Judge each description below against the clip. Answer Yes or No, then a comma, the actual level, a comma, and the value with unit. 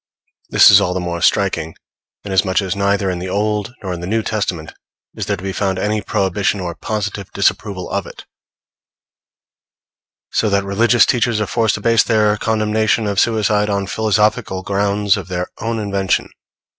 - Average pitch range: No, narrow, 2.2 semitones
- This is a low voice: Yes, low, 100 Hz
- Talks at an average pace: Yes, average, 170 wpm